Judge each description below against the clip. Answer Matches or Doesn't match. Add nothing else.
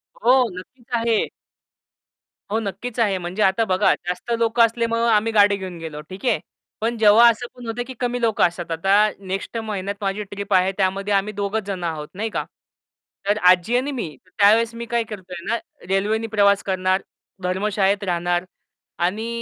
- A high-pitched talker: Matches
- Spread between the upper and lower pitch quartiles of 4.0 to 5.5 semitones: Doesn't match